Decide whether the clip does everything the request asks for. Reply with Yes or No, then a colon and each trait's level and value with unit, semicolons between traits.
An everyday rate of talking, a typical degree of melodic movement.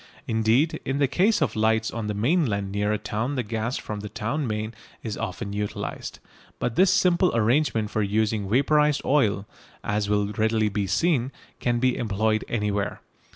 Yes: average, 170 wpm; average, 4.3 semitones